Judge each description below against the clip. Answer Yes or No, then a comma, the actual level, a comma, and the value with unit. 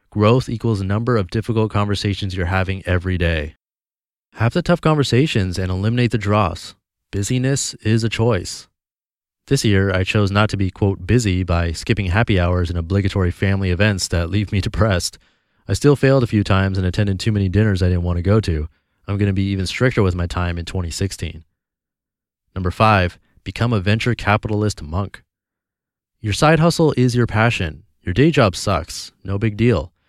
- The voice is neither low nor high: No, low, 100 Hz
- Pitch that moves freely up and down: No, average, 3.7 semitones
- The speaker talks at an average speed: Yes, average, 185 wpm